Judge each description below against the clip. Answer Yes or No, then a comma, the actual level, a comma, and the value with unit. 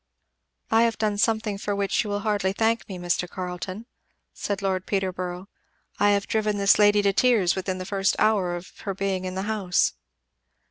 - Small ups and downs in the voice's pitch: Yes, narrow, 2.1 semitones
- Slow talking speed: No, average, 185 wpm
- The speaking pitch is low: No, high, 200 Hz